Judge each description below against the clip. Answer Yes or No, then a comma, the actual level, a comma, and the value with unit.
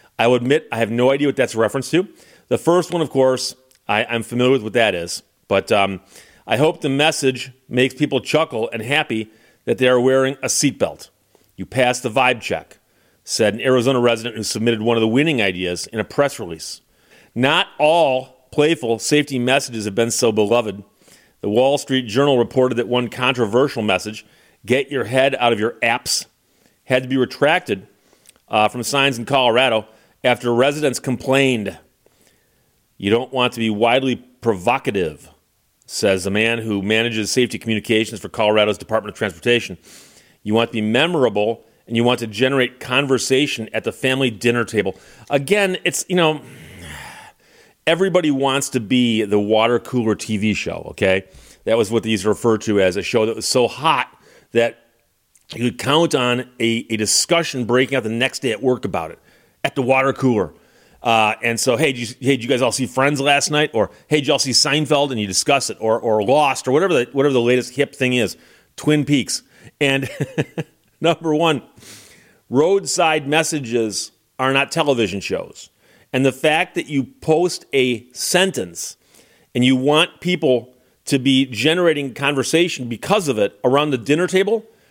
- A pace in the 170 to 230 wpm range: Yes, average, 180 wpm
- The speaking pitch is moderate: No, low, 125 Hz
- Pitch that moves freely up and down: No, average, 3.6 semitones